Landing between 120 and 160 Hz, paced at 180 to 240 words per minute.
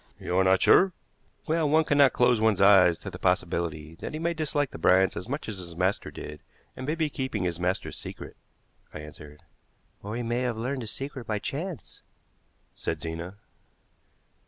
No: low, 110 Hz; average, 185 wpm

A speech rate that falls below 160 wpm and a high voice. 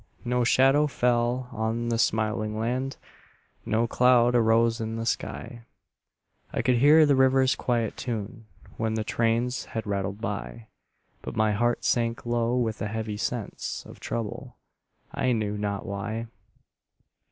No: average, 140 wpm; low, 115 Hz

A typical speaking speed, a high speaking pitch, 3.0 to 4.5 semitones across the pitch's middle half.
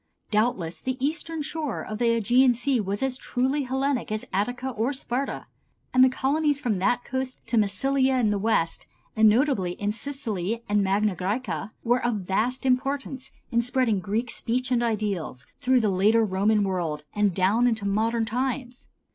Yes: average, 170 wpm; high, 235 Hz; average, 4.0 semitones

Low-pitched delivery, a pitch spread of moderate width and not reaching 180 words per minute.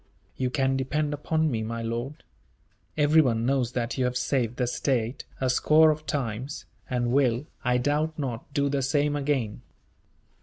Yes: low, 130 Hz; average, 3.2 semitones; average, 160 wpm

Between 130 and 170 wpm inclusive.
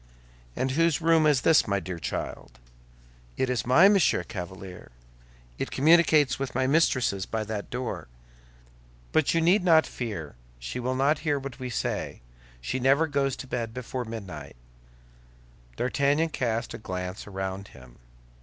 Yes: average, 150 wpm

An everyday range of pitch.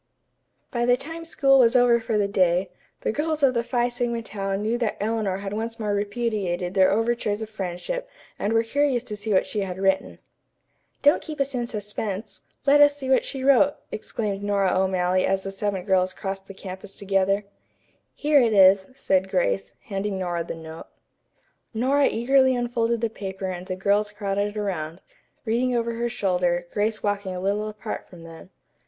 Yes: average, 3.9 semitones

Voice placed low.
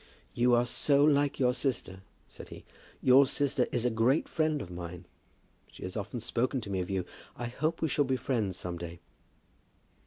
Yes: low, 120 Hz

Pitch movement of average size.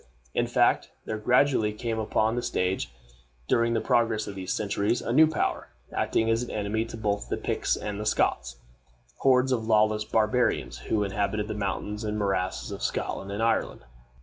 No: narrow, 2.1 semitones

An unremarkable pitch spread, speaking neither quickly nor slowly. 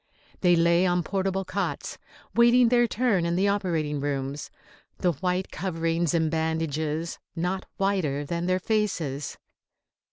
No: average, 3.2 semitones; slow, 130 wpm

